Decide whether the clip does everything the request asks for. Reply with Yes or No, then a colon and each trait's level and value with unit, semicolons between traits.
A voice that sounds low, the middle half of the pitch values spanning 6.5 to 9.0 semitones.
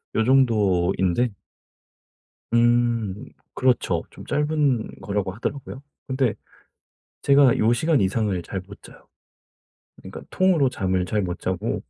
No: low, 115 Hz; wide, 5.4 semitones